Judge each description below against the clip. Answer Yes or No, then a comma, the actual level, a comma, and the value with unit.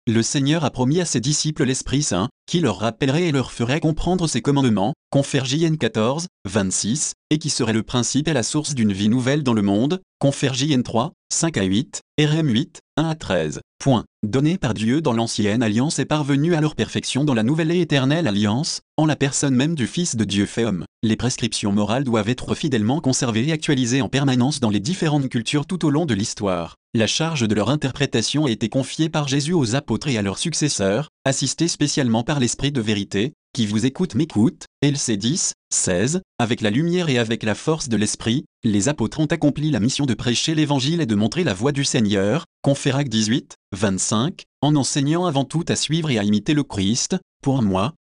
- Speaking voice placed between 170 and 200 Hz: No, low, 135 Hz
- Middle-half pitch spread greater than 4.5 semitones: Yes, average, 5.2 semitones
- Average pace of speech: Yes, average, 205 wpm